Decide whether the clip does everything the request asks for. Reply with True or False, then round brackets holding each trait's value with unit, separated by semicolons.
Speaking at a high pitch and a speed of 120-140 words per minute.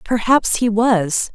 True (220 Hz; 135 wpm)